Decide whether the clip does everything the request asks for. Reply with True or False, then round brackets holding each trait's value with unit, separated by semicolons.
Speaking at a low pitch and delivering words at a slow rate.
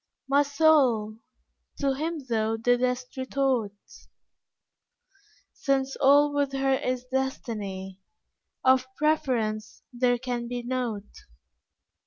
False (255 Hz; 95 wpm)